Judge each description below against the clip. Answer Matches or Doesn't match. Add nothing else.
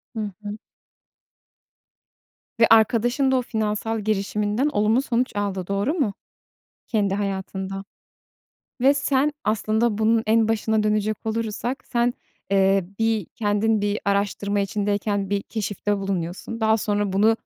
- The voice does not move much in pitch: Matches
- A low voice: Doesn't match